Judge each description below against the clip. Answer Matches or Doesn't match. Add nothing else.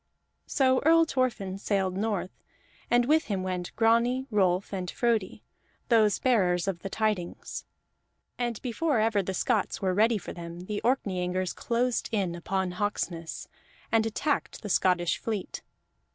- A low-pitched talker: Doesn't match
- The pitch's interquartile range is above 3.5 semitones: Matches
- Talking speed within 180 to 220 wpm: Doesn't match